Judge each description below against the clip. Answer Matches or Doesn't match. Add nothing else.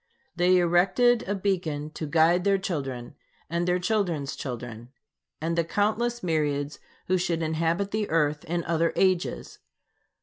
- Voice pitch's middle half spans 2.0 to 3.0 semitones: Doesn't match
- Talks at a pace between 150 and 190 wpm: Doesn't match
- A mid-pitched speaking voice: Matches